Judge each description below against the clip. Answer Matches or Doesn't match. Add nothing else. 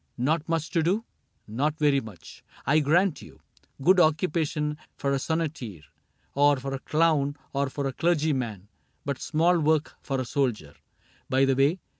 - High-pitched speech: Doesn't match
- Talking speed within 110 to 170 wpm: Matches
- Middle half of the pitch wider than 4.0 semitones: Doesn't match